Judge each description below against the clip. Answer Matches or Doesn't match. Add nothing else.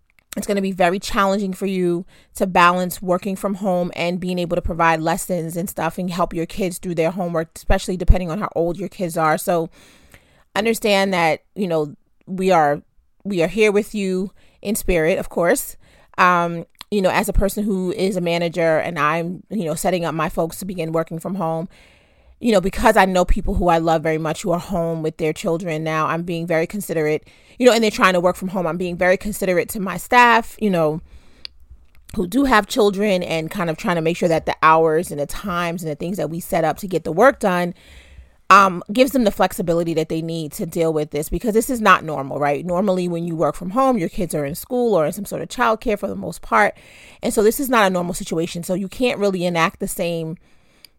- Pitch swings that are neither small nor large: Matches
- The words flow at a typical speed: Doesn't match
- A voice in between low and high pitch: Matches